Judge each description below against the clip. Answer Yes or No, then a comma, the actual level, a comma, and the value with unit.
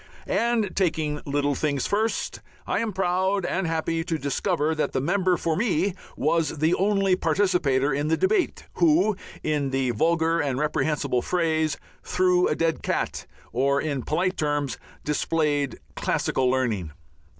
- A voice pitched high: No, medium, 160 Hz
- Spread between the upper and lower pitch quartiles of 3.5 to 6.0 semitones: Yes, average, 4.3 semitones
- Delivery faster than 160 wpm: No, average, 145 wpm